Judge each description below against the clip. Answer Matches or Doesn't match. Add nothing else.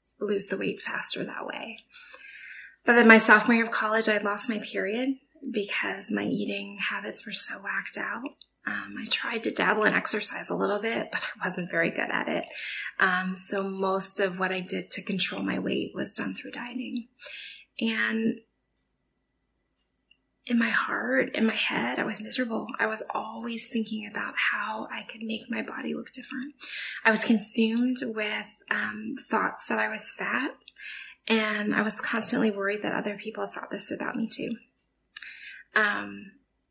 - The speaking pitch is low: Doesn't match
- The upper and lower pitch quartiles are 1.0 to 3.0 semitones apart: Matches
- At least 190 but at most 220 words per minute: Doesn't match